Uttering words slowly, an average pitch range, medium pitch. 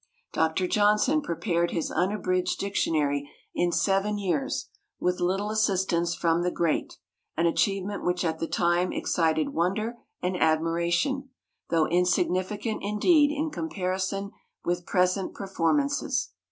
Yes: slow, 120 wpm; average, 3.3 semitones; medium, 180 Hz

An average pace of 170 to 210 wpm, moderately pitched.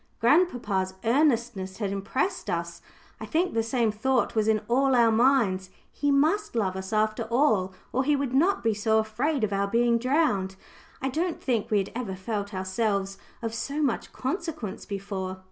No: average, 175 wpm; high, 230 Hz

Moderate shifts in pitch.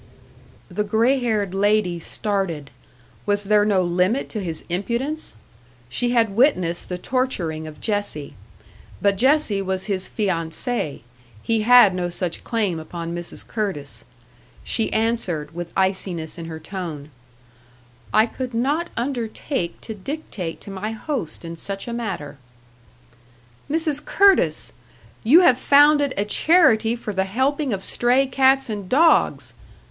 No: wide, 5.8 semitones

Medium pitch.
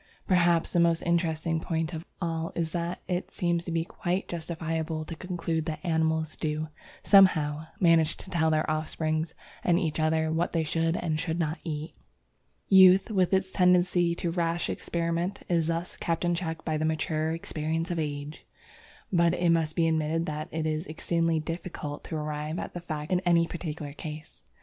Yes: medium, 165 Hz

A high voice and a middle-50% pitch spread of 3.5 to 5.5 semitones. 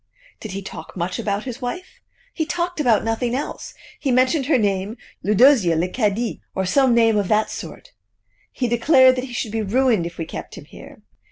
Yes: high, 230 Hz; average, 4.4 semitones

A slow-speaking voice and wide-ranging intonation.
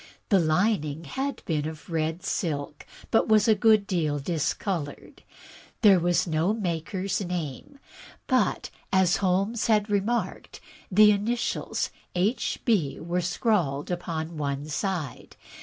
No: slow, 125 wpm; average, 4.8 semitones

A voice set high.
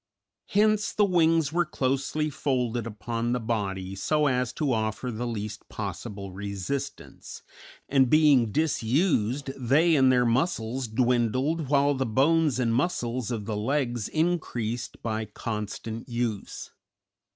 No: low, 125 Hz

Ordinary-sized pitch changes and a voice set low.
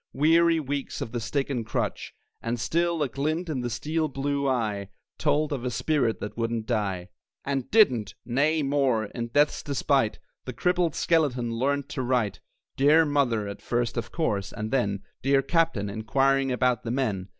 Yes: average, 4.1 semitones; low, 130 Hz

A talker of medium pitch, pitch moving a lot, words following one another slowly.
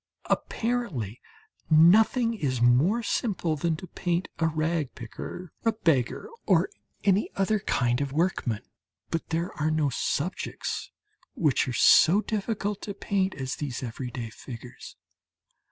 Yes: medium, 160 Hz; wide, 7.3 semitones; slow, 130 wpm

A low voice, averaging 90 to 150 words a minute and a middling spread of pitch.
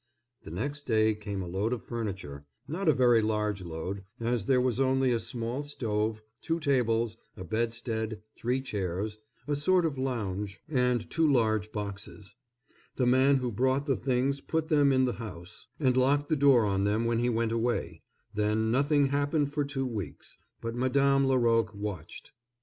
No: low, 120 Hz; average, 170 wpm; average, 4.2 semitones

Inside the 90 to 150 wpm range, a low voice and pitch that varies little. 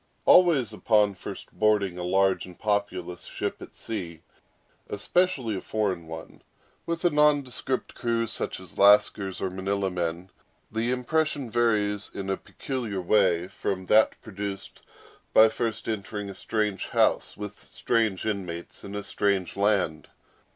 No: average, 140 wpm; low, 105 Hz; average, 3.1 semitones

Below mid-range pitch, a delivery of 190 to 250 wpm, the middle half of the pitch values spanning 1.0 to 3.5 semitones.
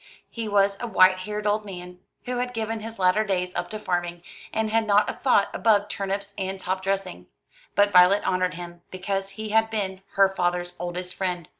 No: high, 195 Hz; average, 195 wpm; average, 2.7 semitones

